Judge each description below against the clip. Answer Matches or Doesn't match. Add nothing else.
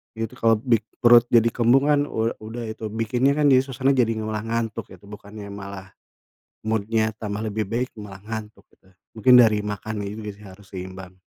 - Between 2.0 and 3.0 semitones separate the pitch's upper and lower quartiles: Matches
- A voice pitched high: Doesn't match